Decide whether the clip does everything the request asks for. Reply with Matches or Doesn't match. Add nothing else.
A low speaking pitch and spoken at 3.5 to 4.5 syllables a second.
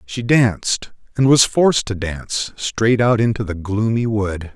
Matches